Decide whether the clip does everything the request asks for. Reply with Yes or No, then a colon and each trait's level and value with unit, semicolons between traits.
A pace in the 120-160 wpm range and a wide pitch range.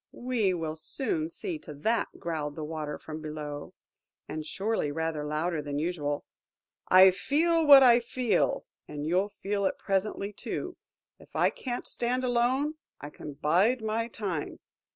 Yes: average, 150 wpm; wide, 7.7 semitones